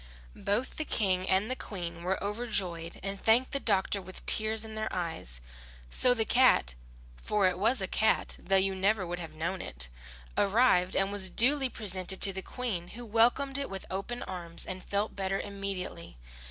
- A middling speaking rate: Yes, average, 180 wpm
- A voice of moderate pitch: No, high, 195 Hz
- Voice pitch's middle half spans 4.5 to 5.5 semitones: No, average, 3.3 semitones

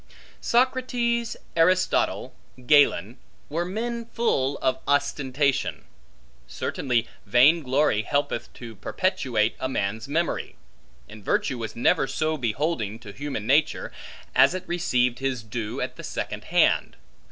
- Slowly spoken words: Yes, slow, 120 wpm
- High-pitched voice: No, low, 135 Hz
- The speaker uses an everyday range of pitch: No, wide, 6.4 semitones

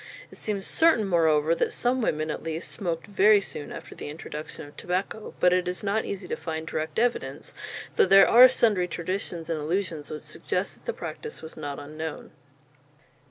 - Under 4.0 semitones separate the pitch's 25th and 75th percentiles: No, average, 4.4 semitones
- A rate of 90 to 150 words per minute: No, average, 185 wpm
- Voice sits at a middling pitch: Yes, medium, 180 Hz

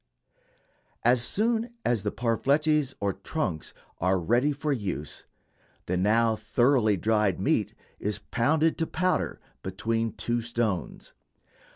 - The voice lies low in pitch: Yes, low, 115 Hz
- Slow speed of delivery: Yes, slow, 115 wpm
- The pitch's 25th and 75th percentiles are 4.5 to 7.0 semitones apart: Yes, wide, 5.6 semitones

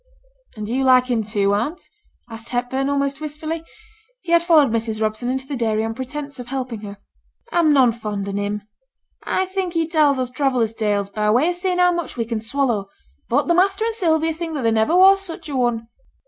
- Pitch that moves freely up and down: Yes, wide, 6.4 semitones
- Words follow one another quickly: Yes, fast, 215 wpm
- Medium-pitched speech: No, very high, 260 Hz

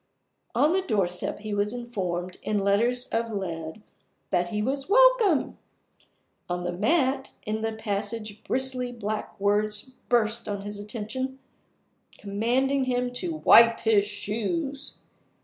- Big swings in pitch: No, average, 4.1 semitones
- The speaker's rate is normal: No, slow, 130 wpm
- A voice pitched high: Yes, high, 220 Hz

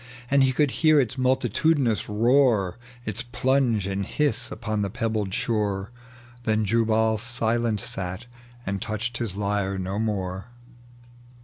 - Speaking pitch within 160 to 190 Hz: No, low, 110 Hz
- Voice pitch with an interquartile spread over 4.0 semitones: No, average, 3.4 semitones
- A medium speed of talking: No, slow, 130 wpm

